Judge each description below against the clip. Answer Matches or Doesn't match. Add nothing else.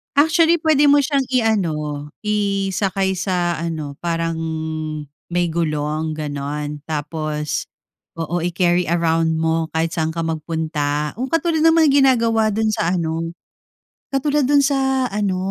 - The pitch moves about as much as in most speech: Doesn't match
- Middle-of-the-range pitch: Matches